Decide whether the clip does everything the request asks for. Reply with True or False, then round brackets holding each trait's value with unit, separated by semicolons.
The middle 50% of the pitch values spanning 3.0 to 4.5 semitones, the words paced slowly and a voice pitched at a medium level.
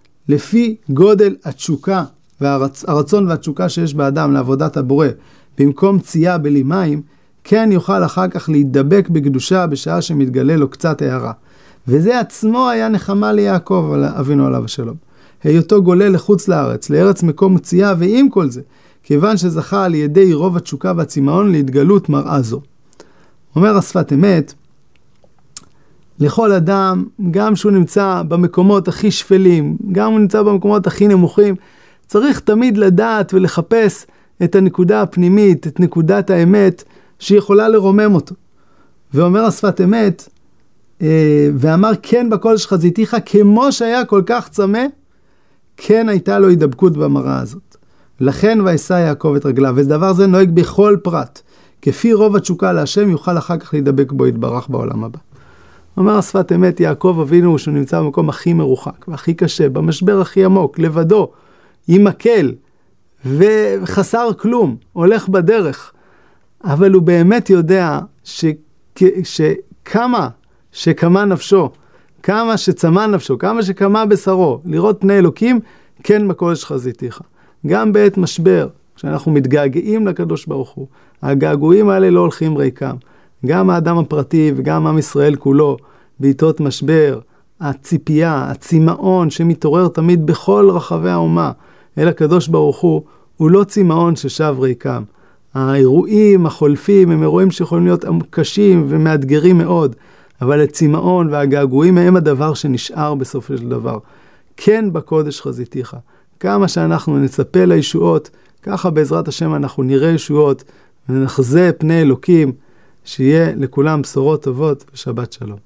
False (5.1 semitones; 130 wpm; 170 Hz)